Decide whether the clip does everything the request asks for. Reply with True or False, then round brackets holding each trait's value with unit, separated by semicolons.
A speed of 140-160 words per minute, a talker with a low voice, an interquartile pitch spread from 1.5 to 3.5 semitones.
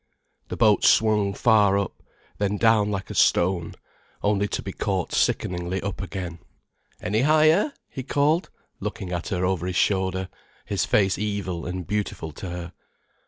True (155 wpm; 100 Hz; 2.7 semitones)